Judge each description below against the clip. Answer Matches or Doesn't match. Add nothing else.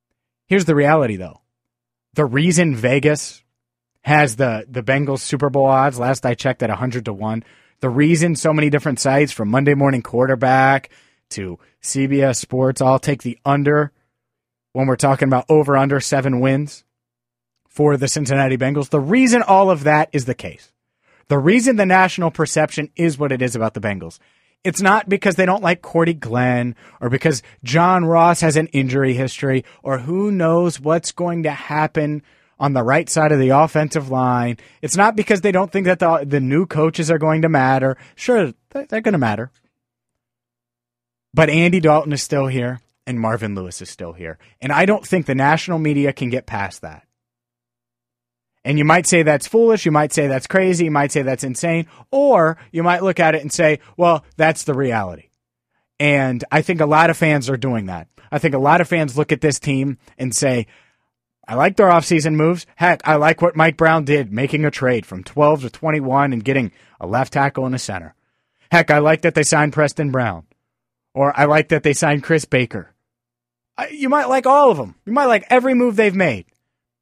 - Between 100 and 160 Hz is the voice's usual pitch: Matches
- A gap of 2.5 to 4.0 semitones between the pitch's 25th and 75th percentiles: Doesn't match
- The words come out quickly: Doesn't match